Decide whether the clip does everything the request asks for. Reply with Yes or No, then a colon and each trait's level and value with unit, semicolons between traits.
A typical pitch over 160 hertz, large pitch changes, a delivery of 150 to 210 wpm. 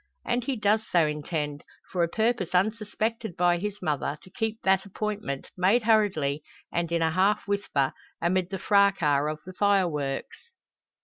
No: medium, 185 Hz; average, 4.7 semitones; average, 160 wpm